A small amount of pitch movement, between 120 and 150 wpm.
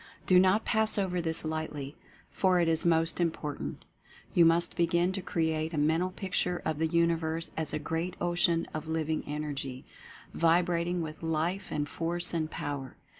No: narrow, 1.9 semitones; average, 170 wpm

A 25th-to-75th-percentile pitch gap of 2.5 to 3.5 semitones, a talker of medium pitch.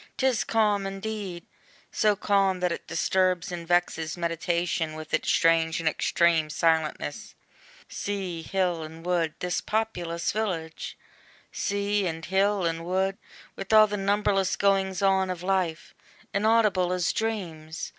Yes: average, 3.2 semitones; medium, 180 Hz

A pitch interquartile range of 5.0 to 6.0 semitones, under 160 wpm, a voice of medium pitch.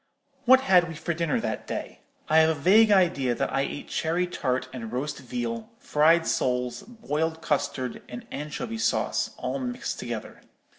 No: wide, 5.5 semitones; average, 165 wpm; medium, 155 Hz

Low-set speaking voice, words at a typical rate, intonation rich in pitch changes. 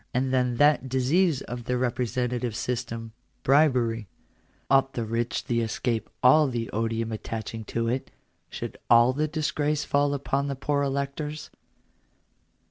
No: low, 125 Hz; average, 145 wpm; average, 3.3 semitones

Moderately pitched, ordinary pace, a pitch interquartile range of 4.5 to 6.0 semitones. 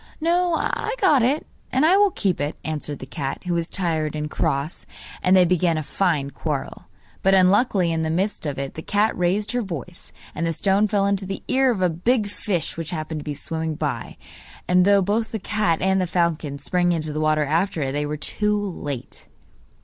No: medium, 180 Hz; fast, 210 wpm; average, 4.8 semitones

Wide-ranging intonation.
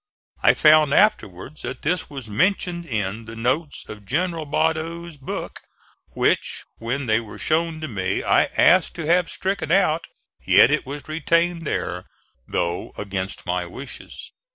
Yes: wide, 6.7 semitones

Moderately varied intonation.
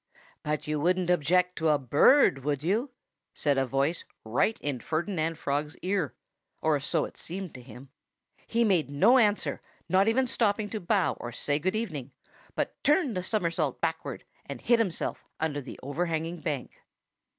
No: wide, 5.8 semitones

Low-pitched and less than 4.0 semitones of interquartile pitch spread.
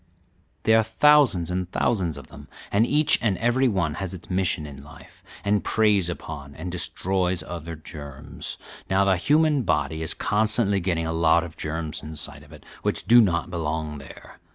No: very low, 90 Hz; average, 4.9 semitones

